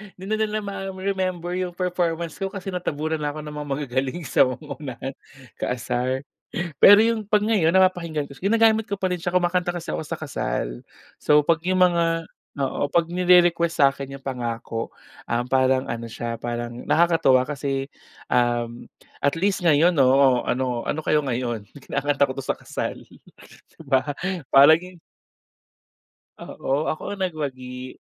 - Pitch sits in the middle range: Yes, medium, 155 Hz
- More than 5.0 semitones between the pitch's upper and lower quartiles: Yes, wide, 5.4 semitones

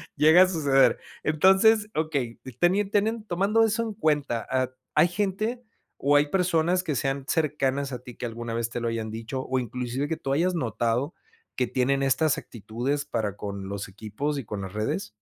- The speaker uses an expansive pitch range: Yes, wide, 6.8 semitones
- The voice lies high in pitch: No, medium, 140 Hz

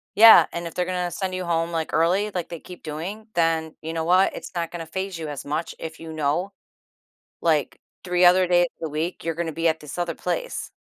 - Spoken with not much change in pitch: Yes, narrow, 2.1 semitones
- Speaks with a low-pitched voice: No, medium, 170 Hz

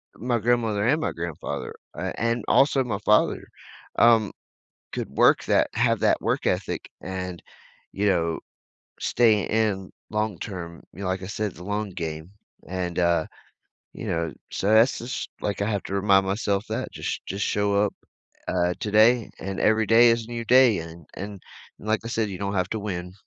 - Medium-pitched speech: No, low, 100 Hz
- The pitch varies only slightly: No, average, 3.3 semitones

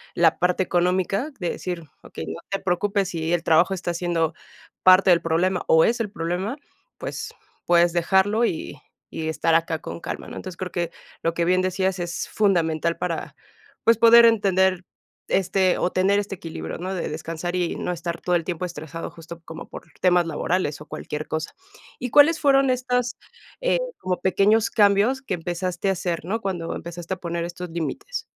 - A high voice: No, medium, 180 Hz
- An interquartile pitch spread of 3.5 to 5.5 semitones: No, average, 2.7 semitones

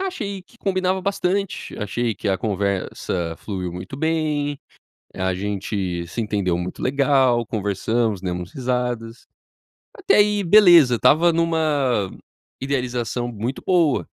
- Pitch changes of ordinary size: No, wide, 8.4 semitones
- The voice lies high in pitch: No, low, 125 Hz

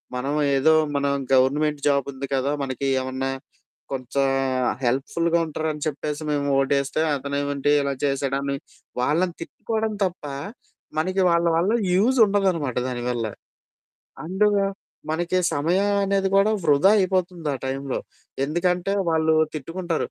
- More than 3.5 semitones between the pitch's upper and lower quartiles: Yes, average, 4.5 semitones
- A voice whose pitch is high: No, medium, 150 Hz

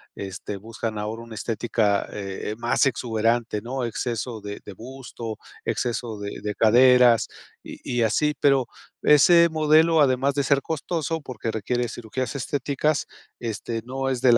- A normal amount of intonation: Yes, average, 3.4 semitones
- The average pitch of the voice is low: Yes, low, 120 Hz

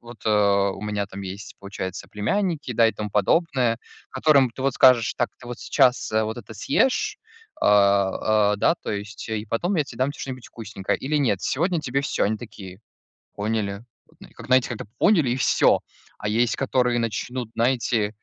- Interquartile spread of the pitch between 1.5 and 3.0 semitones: No, average, 4.0 semitones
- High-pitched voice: No, low, 115 Hz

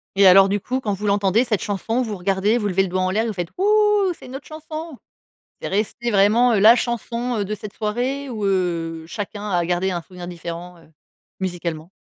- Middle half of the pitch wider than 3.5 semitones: Yes, average, 4.4 semitones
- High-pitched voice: Yes, high, 200 Hz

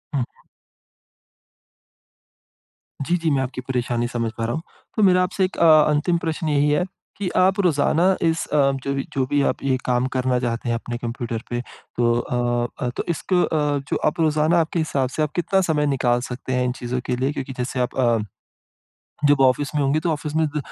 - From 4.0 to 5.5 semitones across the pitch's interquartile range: Yes, average, 4.3 semitones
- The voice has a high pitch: No, medium, 140 Hz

